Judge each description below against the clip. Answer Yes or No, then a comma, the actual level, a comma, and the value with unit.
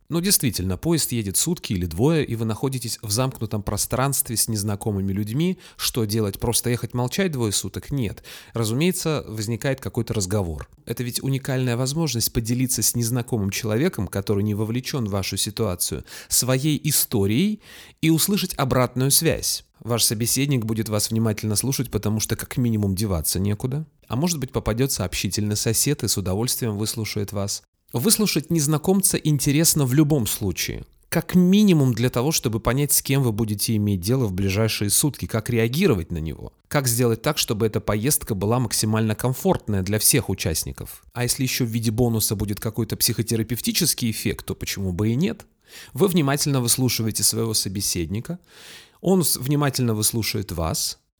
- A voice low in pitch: Yes, low, 115 Hz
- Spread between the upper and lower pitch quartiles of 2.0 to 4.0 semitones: No, average, 4.5 semitones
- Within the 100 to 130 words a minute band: No, average, 155 wpm